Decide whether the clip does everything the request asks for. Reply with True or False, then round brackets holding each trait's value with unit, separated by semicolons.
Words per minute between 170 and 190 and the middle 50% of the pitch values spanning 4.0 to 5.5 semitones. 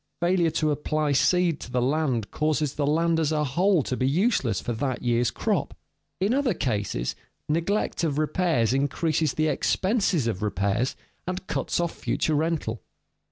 False (160 wpm; 5.1 semitones)